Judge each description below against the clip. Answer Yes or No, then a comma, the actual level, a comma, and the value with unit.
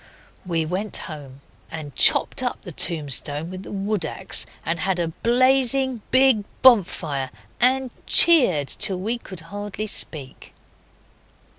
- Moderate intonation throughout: No, wide, 7.2 semitones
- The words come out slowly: Yes, slow, 130 wpm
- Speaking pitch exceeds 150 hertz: Yes, high, 190 Hz